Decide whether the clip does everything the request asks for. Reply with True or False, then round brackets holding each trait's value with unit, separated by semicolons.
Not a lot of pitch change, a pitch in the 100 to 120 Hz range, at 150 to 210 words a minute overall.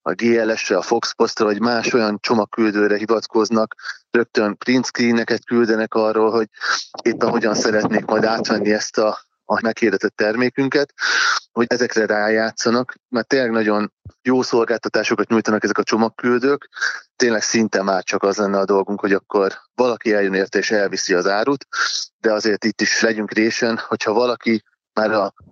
True (1.9 semitones; 110 Hz; 155 wpm)